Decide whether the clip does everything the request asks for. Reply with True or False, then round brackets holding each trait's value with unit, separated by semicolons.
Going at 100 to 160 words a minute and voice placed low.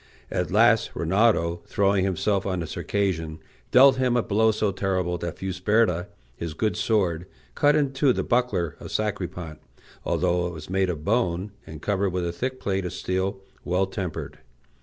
False (170 wpm; 95 Hz)